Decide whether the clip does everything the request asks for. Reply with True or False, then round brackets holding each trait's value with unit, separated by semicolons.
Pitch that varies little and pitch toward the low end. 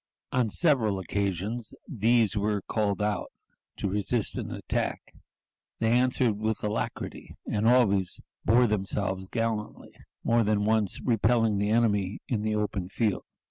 True (2.2 semitones; 105 Hz)